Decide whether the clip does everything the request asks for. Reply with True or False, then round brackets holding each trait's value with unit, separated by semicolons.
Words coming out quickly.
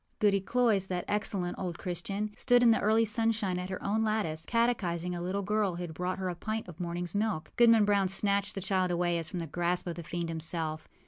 True (225 wpm)